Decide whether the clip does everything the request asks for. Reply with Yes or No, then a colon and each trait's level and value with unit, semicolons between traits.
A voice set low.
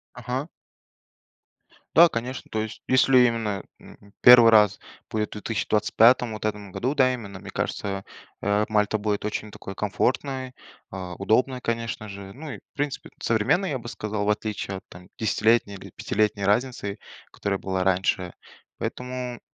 Yes: low, 110 Hz